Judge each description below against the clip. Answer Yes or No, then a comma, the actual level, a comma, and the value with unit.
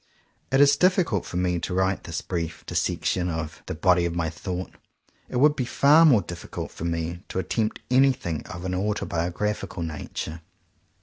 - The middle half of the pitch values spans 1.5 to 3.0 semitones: No, wide, 5.4 semitones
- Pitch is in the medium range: No, very low, 90 Hz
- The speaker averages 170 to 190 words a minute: Yes, average, 175 wpm